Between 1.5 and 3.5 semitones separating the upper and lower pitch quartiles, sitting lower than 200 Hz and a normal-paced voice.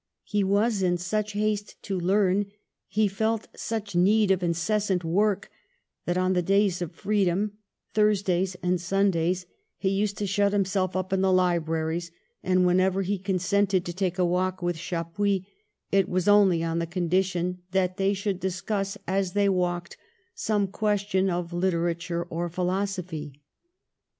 Yes: narrow, 2.4 semitones; medium, 185 Hz; average, 160 wpm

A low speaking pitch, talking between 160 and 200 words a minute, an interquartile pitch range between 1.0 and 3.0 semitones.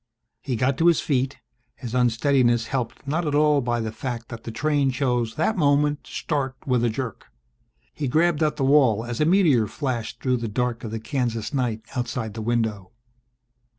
No: low, 125 Hz; average, 190 wpm; average, 3.8 semitones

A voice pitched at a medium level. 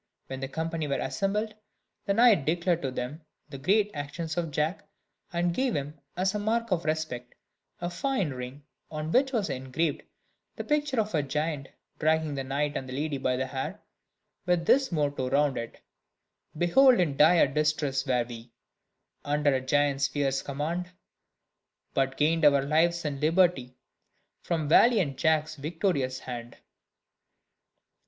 Yes: medium, 150 Hz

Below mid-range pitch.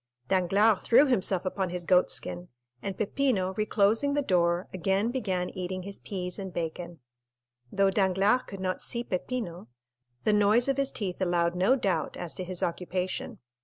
No: high, 190 Hz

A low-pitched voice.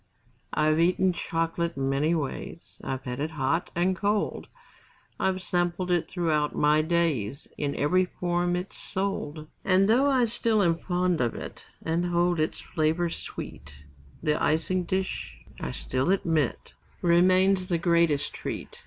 No: medium, 170 Hz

